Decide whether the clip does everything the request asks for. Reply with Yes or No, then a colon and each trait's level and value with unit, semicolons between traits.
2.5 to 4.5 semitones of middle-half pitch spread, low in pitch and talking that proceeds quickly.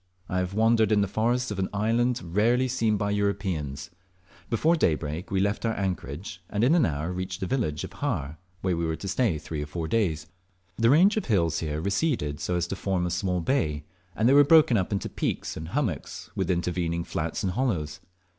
No: wide, 5.5 semitones; very low, 95 Hz; fast, 210 wpm